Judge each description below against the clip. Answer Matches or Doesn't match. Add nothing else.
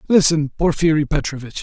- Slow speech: Matches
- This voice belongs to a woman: Doesn't match